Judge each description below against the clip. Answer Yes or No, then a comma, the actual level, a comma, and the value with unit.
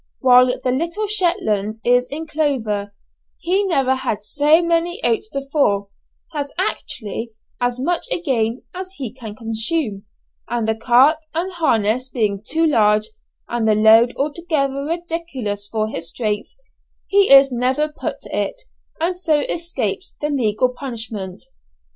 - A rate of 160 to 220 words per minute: No, average, 140 wpm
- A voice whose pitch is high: Yes, very high, 260 Hz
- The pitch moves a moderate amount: No, wide, 6.6 semitones